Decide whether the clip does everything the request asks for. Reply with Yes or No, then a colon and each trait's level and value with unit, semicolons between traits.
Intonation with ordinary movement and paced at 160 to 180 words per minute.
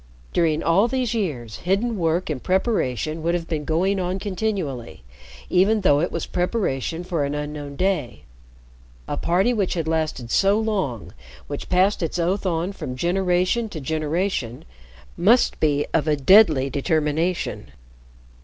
No: average, 4.7 semitones; average, 145 wpm